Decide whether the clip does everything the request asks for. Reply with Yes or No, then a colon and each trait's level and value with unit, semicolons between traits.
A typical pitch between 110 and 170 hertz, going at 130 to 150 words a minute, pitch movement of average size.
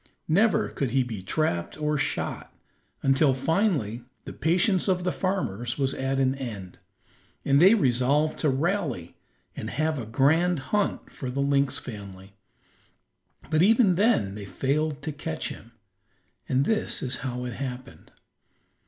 Yes: medium, 140 Hz; average, 145 wpm; average, 4.7 semitones